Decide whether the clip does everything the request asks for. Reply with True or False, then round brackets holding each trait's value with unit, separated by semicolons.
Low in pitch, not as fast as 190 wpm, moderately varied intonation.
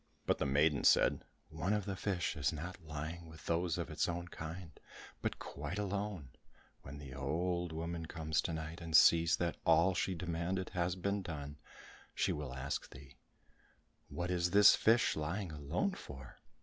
True (85 Hz; 170 wpm; 3.1 semitones)